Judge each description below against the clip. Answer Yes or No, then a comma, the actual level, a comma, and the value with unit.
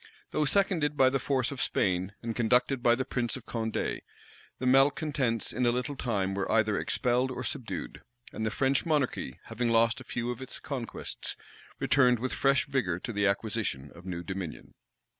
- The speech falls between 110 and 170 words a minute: No, average, 180 wpm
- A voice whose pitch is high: No, low, 120 Hz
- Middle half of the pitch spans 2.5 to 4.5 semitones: Yes, average, 3.6 semitones